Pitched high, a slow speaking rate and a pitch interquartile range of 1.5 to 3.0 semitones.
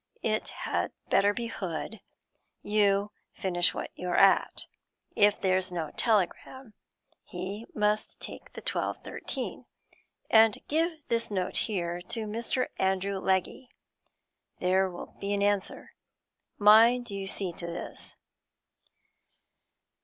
Yes: high, 200 Hz; slow, 115 wpm; average, 2.7 semitones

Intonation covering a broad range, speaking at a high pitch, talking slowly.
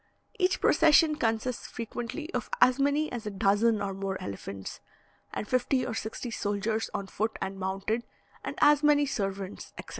No: wide, 5.7 semitones; high, 225 Hz; average, 160 wpm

